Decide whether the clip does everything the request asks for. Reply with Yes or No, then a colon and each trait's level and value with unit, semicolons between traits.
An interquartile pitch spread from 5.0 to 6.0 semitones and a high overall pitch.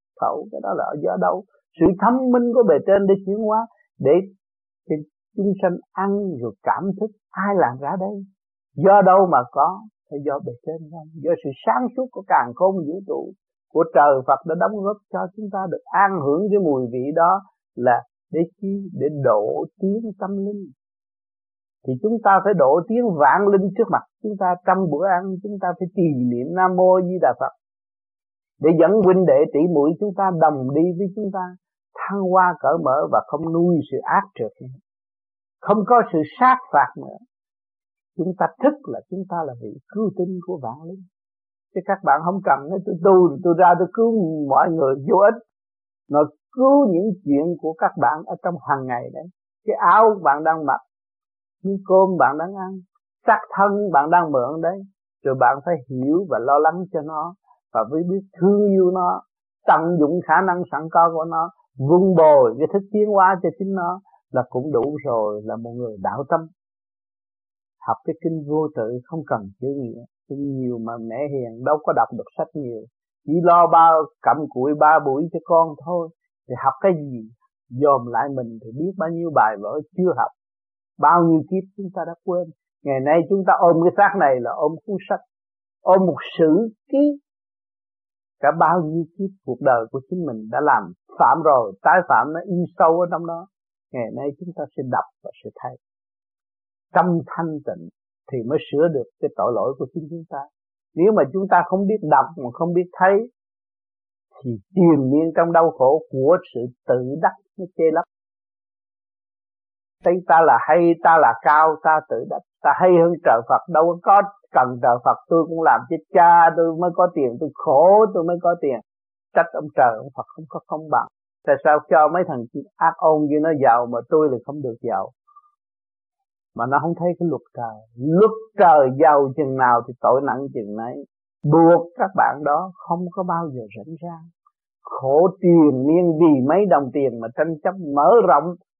No: average, 5.3 semitones; medium, 170 Hz